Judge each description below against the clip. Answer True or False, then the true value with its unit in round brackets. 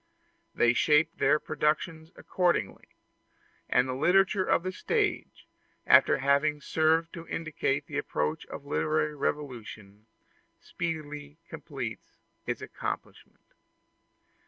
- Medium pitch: True (150 Hz)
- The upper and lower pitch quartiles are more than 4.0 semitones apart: False (3.6 semitones)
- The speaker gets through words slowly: True (100 wpm)